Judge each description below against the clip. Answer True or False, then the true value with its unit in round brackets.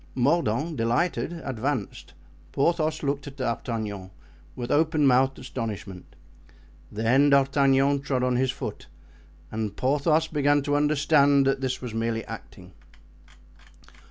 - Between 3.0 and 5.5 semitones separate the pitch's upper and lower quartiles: True (3.6 semitones)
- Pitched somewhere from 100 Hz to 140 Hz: True (135 Hz)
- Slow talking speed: True (115 wpm)